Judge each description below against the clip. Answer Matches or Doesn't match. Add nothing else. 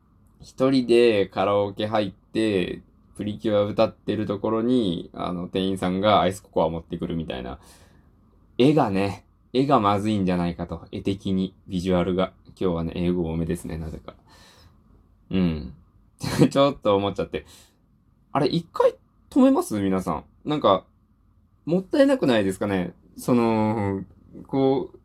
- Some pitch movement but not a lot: Matches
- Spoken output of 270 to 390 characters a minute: Matches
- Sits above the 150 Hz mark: Doesn't match